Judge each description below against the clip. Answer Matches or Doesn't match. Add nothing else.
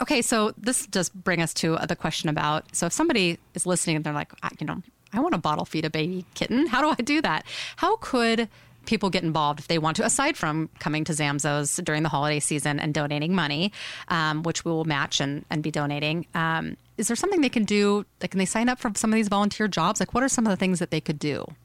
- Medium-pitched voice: Matches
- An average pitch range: Doesn't match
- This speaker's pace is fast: Matches